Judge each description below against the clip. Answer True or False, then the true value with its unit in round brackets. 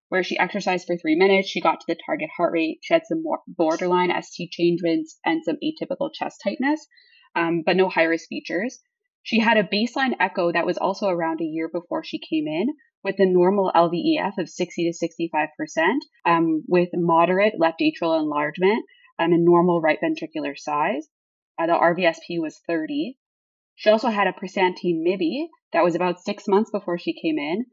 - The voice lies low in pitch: False (185 Hz)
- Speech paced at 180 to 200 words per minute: True (190 wpm)